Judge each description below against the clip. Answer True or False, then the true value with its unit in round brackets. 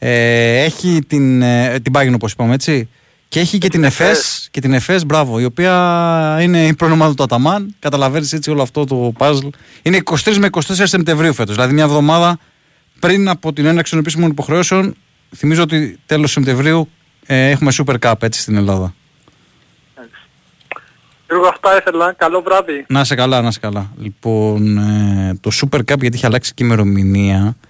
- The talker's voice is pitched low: False (145 Hz)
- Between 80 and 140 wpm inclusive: False (155 wpm)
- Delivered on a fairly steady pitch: False (5.3 semitones)